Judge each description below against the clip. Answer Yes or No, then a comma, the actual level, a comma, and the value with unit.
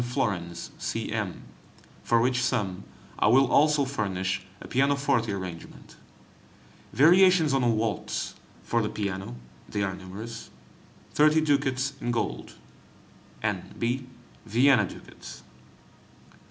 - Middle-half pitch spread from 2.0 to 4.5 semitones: No, wide, 5.4 semitones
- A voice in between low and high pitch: No, low, 120 Hz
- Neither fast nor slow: No, slow, 120 wpm